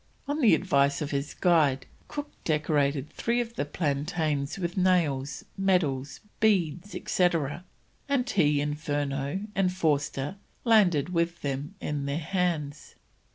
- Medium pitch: Yes, medium, 155 Hz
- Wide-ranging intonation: No, average, 4.4 semitones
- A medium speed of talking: No, slow, 125 wpm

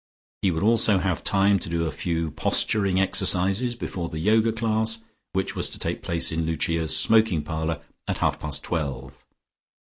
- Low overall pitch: Yes, very low, 90 Hz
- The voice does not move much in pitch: No, average, 4.7 semitones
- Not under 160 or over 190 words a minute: Yes, average, 175 wpm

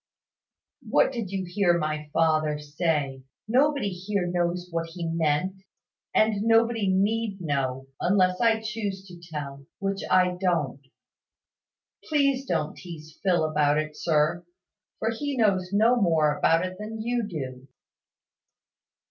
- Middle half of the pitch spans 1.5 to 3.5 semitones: No, average, 5.3 semitones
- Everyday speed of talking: No, slow, 130 wpm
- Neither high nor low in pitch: Yes, medium, 180 Hz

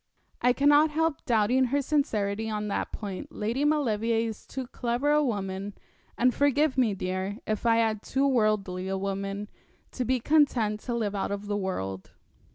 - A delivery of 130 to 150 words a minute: No, average, 170 wpm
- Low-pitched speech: No, high, 225 Hz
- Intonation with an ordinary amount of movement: Yes, average, 4.6 semitones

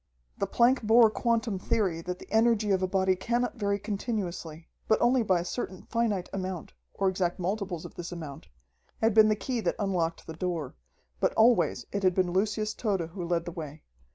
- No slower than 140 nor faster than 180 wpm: No, average, 195 wpm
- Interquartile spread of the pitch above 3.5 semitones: Yes, average, 3.9 semitones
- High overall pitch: Yes, high, 195 Hz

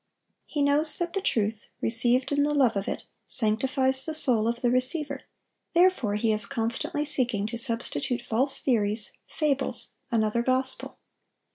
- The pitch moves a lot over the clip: No, average, 4.0 semitones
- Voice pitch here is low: No, very high, 255 Hz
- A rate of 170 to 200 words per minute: No, average, 150 wpm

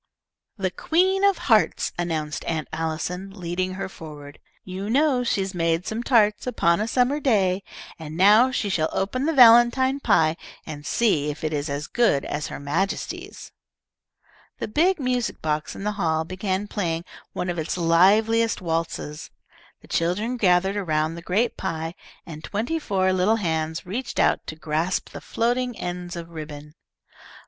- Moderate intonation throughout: No, wide, 5.8 semitones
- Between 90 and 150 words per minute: No, average, 160 wpm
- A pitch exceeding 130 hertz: Yes, medium, 185 Hz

